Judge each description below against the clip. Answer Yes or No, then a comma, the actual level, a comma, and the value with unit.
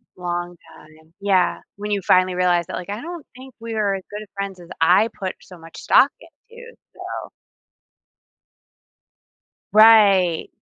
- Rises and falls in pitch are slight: No, average, 4.0 semitones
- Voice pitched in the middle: No, high, 195 Hz